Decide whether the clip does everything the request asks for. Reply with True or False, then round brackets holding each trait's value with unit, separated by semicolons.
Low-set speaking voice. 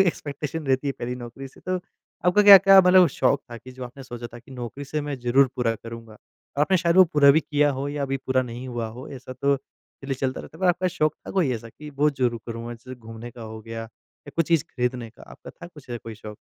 True (130 Hz)